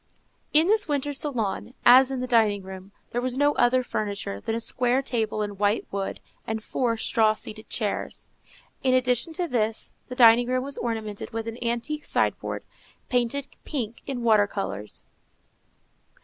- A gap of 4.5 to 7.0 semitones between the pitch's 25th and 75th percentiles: No, average, 3.1 semitones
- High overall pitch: Yes, high, 235 Hz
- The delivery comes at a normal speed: Yes, average, 165 wpm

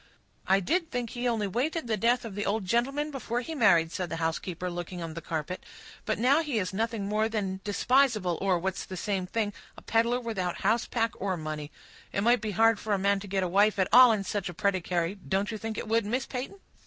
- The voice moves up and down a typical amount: Yes, average, 3.9 semitones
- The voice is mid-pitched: No, high, 205 Hz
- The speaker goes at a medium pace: No, fast, 230 wpm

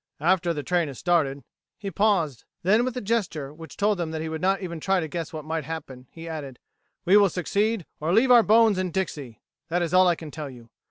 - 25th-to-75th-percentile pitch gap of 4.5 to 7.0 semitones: No, average, 4.0 semitones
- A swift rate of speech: Yes, fast, 235 wpm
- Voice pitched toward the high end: No, medium, 170 Hz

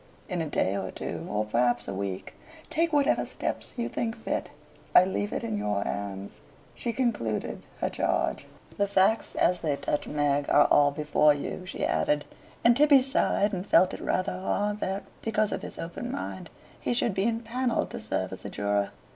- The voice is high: No, medium, 180 Hz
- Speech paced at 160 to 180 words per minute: No, average, 190 wpm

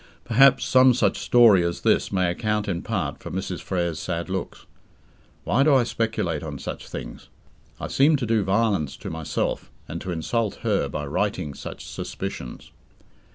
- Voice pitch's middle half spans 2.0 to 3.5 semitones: No, wide, 5.4 semitones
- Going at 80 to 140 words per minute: No, average, 165 wpm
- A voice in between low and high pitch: No, very low, 95 Hz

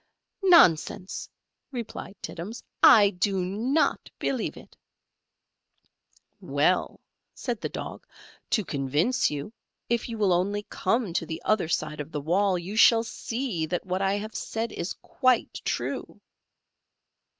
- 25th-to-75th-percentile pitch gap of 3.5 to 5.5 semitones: Yes, average, 4.7 semitones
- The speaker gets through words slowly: Yes, slow, 130 wpm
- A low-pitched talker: No, high, 200 Hz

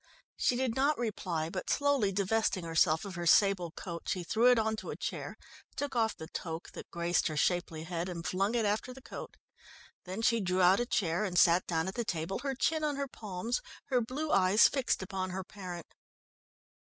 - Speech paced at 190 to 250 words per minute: Yes, fast, 205 wpm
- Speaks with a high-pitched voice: Yes, high, 195 Hz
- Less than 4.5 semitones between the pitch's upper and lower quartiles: No, average, 5.2 semitones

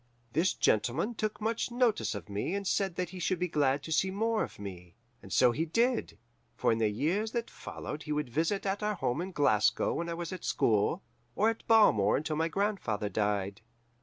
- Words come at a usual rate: No, fast, 210 wpm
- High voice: No, medium, 165 Hz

